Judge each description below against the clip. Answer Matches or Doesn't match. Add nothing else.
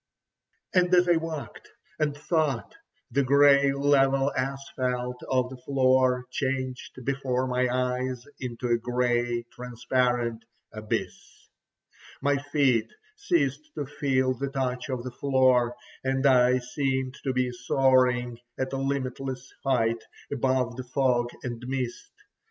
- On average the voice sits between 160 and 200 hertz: Doesn't match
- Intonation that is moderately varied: Doesn't match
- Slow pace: Matches